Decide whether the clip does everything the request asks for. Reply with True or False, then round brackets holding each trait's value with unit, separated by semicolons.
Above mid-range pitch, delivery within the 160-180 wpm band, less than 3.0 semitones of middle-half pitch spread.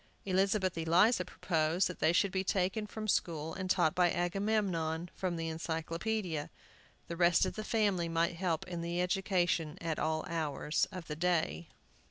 False (175 Hz; 165 wpm; 2.6 semitones)